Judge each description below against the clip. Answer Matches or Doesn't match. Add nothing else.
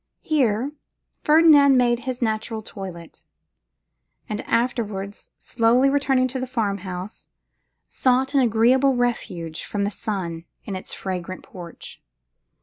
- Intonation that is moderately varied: Matches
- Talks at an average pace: Doesn't match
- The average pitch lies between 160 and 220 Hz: Doesn't match